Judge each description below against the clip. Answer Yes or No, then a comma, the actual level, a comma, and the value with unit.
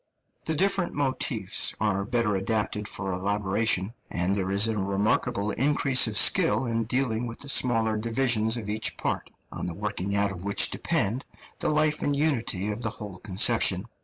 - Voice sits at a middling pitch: No, low, 110 Hz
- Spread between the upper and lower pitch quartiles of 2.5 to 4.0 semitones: Yes, average, 3.6 semitones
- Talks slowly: No, average, 170 wpm